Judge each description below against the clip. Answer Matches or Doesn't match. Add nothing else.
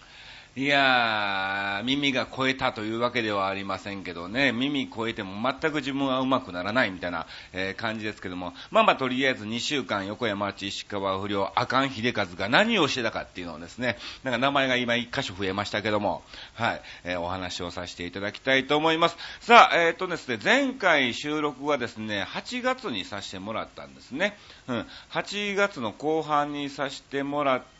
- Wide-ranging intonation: Matches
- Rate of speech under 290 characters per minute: Doesn't match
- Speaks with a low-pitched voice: Matches